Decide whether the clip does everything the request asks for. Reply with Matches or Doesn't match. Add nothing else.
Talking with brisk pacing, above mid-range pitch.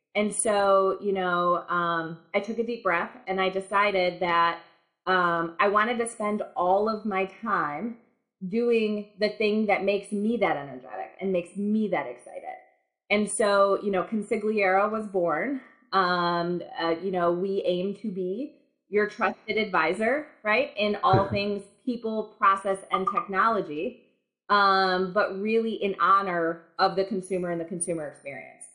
Doesn't match